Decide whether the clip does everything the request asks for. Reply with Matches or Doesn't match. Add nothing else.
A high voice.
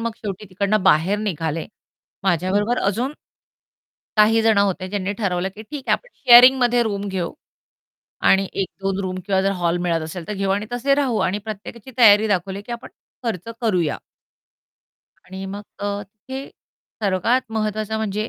Matches